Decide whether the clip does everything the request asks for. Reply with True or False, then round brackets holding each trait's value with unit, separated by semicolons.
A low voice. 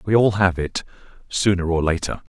True (95 Hz)